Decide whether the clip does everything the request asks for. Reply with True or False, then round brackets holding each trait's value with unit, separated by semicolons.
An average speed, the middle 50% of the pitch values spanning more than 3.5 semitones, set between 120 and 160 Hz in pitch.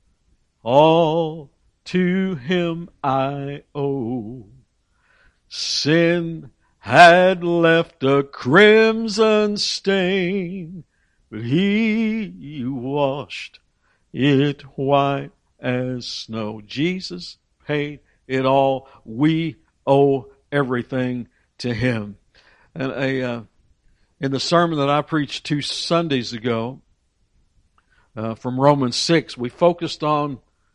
False (90 wpm; 5.0 semitones; 140 Hz)